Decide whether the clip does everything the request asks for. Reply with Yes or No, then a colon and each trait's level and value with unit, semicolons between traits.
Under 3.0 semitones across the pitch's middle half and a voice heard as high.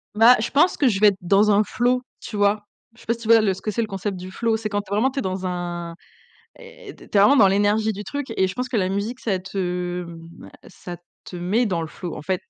No: average, 3.7 semitones; high, 205 Hz